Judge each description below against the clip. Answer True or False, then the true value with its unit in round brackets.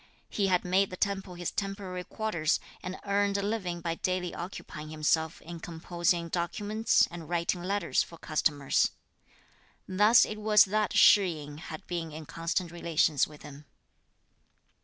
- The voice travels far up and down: False (3.4 semitones)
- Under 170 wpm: True (150 wpm)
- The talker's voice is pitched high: False (175 Hz)